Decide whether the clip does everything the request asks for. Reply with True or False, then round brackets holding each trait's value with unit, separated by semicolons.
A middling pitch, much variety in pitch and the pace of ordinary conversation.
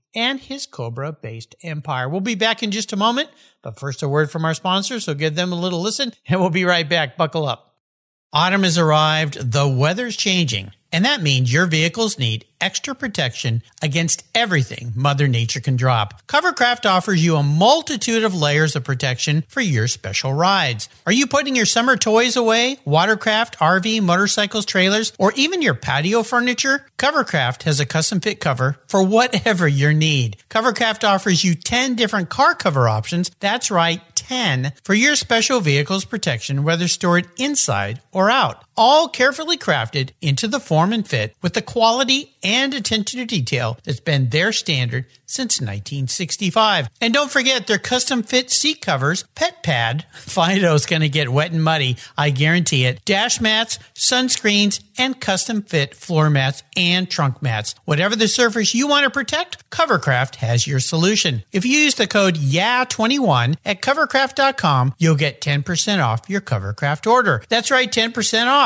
True (180 Hz; 8.1 semitones; 170 wpm)